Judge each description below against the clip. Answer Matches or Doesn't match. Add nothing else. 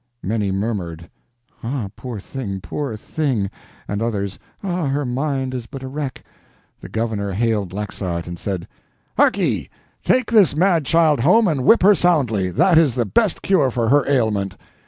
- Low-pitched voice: Matches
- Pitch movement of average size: Doesn't match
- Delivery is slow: Doesn't match